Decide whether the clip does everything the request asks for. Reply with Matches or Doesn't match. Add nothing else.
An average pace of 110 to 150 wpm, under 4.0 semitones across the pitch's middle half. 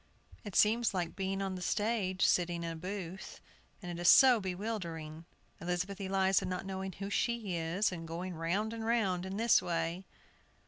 Doesn't match